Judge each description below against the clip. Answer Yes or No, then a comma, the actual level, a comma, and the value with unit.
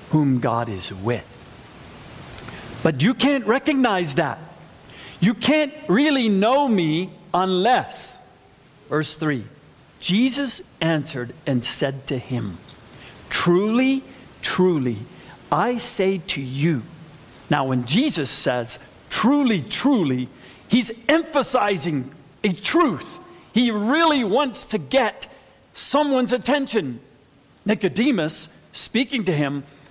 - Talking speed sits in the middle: No, slow, 100 wpm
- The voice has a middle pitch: Yes, medium, 180 Hz